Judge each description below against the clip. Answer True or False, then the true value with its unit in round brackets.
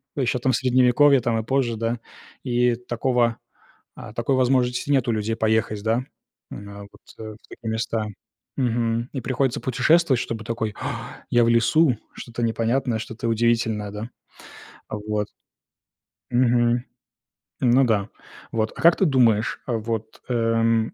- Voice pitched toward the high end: False (115 Hz)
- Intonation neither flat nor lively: False (2.0 semitones)